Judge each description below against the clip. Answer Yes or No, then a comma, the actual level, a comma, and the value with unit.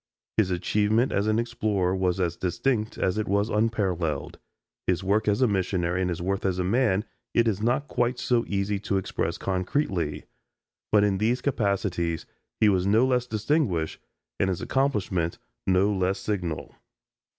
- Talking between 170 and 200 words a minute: No, average, 160 wpm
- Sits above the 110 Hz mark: No, low, 100 Hz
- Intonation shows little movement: No, average, 3.3 semitones